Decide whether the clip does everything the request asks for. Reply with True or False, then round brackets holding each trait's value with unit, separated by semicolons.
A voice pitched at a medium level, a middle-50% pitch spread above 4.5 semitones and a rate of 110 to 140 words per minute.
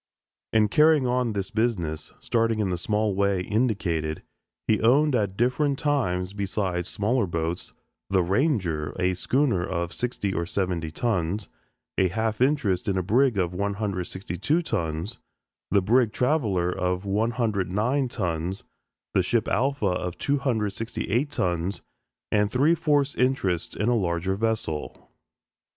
False (100 Hz; 5.2 semitones; 135 wpm)